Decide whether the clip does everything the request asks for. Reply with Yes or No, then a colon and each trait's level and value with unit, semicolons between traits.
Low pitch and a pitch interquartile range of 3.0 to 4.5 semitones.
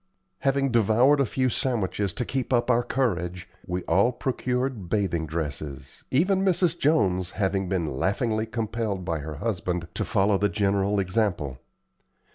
No: low, 105 Hz; wide, 5.6 semitones